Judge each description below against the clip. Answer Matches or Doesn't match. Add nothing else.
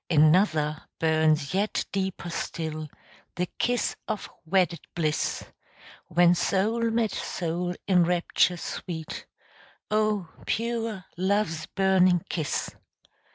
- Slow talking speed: Matches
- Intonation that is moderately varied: Matches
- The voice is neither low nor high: Matches